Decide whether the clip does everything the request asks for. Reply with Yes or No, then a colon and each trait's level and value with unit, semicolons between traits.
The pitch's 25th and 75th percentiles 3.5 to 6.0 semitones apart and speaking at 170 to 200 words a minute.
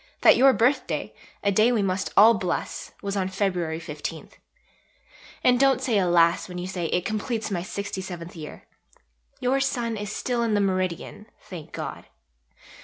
No: average, 4.4 semitones; average, 160 wpm